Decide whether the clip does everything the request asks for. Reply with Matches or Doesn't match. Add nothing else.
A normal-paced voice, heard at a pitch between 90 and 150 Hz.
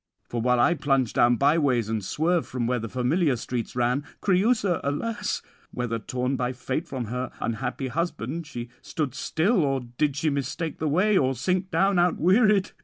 Matches